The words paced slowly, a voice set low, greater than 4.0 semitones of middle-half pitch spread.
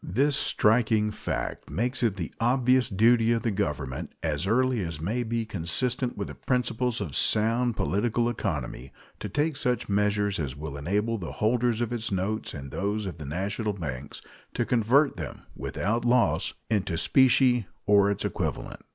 No: average, 165 wpm; low, 110 Hz; average, 4.4 semitones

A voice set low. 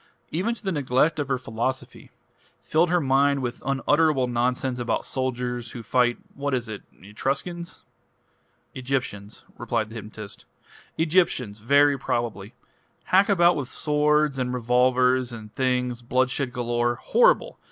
Yes: low, 130 Hz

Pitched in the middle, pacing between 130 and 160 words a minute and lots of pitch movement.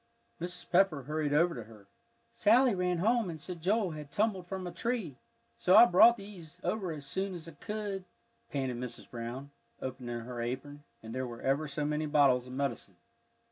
No: medium, 155 Hz; average, 180 wpm; wide, 6.4 semitones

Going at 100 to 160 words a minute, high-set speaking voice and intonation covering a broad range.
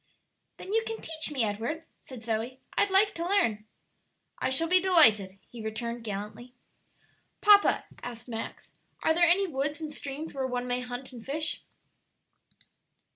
Yes: average, 155 wpm; very high, 265 Hz; wide, 6.0 semitones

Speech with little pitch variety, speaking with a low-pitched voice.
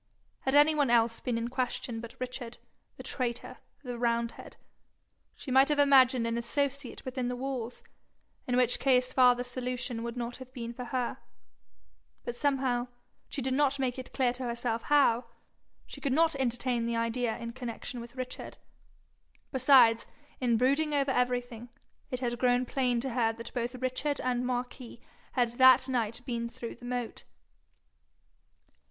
No: narrow, 1.8 semitones; very high, 250 Hz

